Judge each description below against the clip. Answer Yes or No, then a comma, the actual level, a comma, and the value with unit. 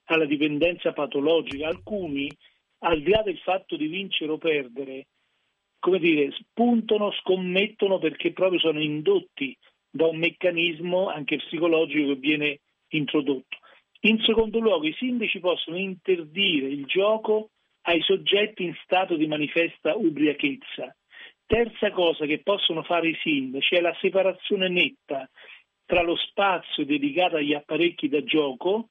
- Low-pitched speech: No, medium, 175 Hz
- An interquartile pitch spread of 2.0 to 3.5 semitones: No, average, 4.6 semitones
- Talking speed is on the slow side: No, average, 130 wpm